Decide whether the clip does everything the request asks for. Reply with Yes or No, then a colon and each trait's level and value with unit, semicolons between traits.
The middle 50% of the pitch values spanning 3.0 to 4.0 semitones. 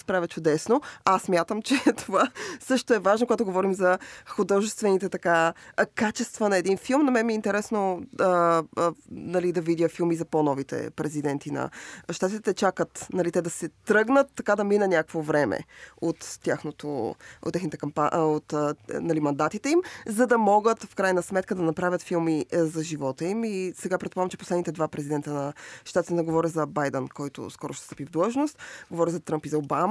No: average, 4.6 semitones